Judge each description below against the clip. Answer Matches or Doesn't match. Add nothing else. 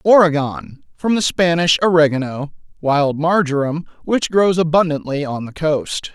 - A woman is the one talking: Doesn't match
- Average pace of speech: Doesn't match